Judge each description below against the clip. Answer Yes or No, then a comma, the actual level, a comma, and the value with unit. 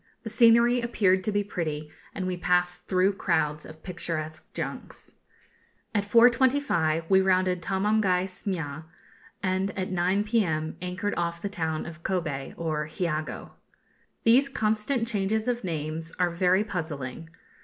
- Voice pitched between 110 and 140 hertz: No, medium, 185 Hz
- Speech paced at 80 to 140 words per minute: Yes, slow, 135 wpm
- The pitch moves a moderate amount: Yes, average, 4.2 semitones